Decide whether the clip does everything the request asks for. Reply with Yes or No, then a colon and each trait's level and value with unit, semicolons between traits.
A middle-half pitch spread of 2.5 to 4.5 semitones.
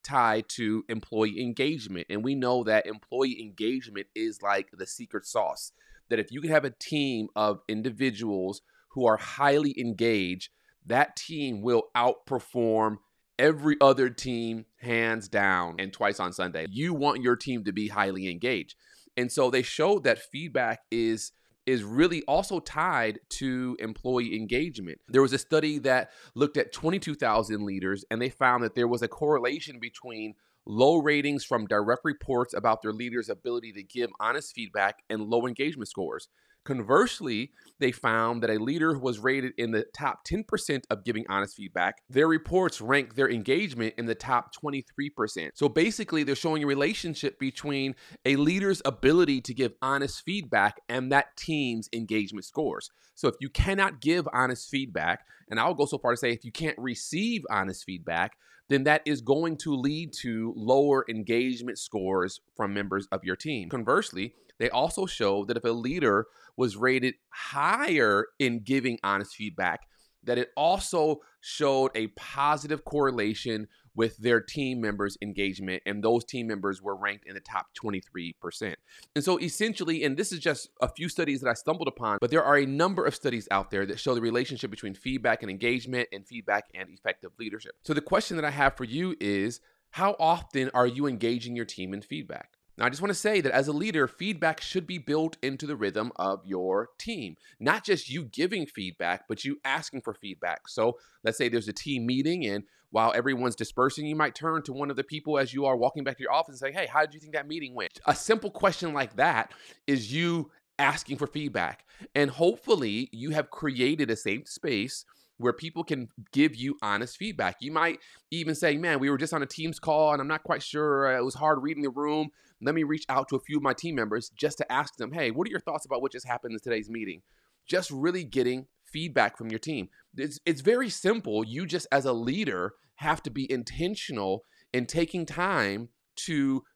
No: average, 5.0 semitones